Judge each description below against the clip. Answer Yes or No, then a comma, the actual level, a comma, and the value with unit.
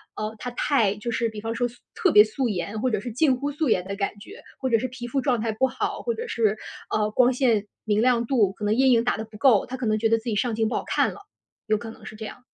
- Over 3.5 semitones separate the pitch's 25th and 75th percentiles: No, average, 3.1 semitones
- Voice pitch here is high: Yes, high, 230 Hz